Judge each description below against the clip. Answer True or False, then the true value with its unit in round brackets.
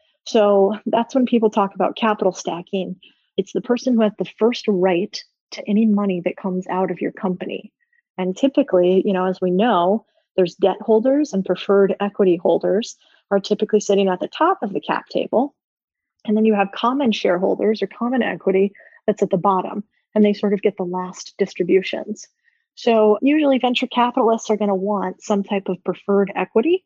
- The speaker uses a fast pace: False (185 wpm)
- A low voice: False (205 Hz)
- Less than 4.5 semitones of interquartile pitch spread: True (3.7 semitones)